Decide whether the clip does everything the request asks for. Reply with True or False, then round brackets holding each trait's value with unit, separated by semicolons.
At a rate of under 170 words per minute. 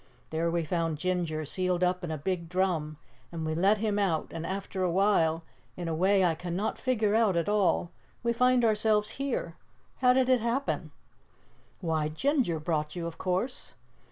False (175 wpm)